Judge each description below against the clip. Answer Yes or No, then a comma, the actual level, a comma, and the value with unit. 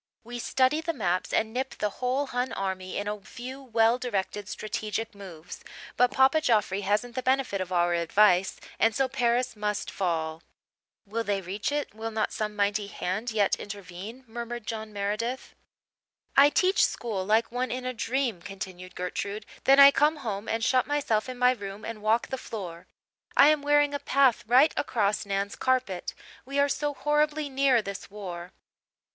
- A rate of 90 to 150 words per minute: No, average, 175 wpm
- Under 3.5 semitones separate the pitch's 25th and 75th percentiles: No, average, 4.4 semitones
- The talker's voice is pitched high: Yes, high, 225 Hz